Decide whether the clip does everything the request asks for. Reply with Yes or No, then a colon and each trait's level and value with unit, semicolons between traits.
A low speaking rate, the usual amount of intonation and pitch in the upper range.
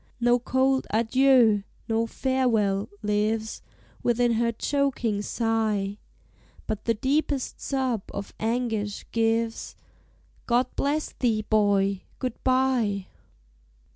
Yes: slow, 100 wpm; average, 3.3 semitones; high, 230 Hz